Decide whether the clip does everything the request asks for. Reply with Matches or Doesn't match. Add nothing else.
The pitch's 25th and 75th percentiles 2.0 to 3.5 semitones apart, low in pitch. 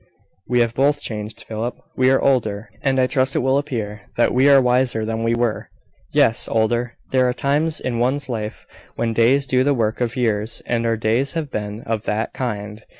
Matches